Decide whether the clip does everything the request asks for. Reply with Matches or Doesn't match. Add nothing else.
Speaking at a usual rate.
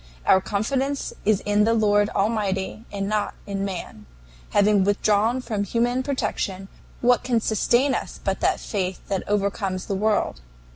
Matches